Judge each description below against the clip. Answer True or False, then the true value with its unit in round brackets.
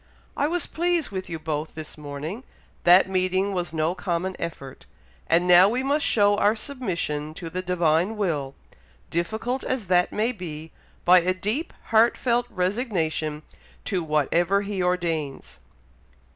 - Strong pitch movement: False (4.6 semitones)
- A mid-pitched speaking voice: True (180 Hz)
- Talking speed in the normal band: True (145 wpm)